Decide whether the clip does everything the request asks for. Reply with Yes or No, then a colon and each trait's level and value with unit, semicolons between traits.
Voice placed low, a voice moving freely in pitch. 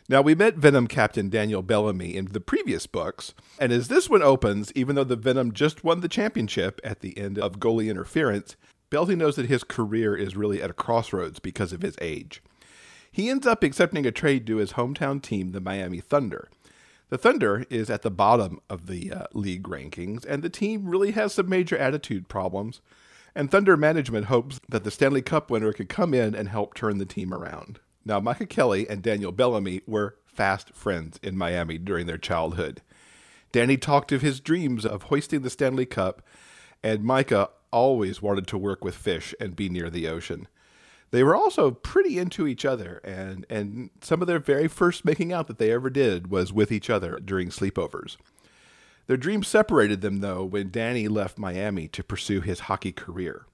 Yes: low, 110 Hz; wide, 6.4 semitones